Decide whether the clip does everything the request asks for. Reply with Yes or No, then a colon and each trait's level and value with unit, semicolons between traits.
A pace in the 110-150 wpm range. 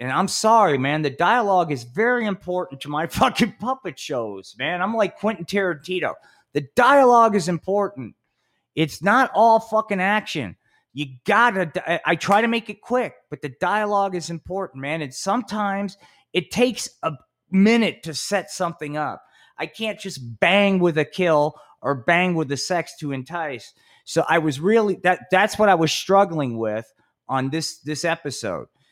No: average, 170 wpm